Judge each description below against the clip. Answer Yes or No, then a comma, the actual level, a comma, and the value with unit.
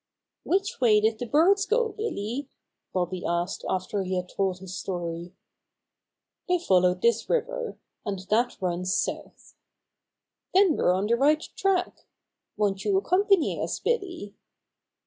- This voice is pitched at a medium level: No, high, 230 Hz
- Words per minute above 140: No, slow, 135 wpm